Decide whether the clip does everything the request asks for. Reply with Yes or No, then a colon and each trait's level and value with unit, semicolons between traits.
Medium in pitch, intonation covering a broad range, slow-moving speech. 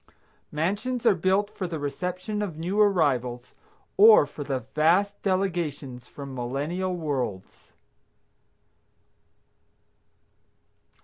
Yes: medium, 170 Hz; wide, 5.8 semitones; slow, 90 wpm